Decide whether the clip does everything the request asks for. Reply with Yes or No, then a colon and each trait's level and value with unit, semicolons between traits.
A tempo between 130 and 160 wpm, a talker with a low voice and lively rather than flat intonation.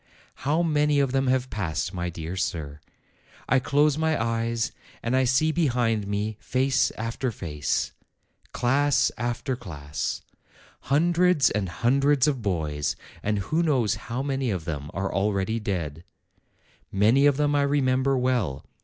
Yes: average, 145 wpm; low, 120 Hz; wide, 6.2 semitones